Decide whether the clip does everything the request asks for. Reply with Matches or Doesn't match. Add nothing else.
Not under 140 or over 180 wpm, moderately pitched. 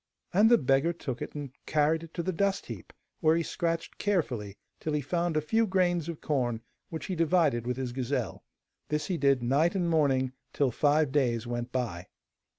Doesn't match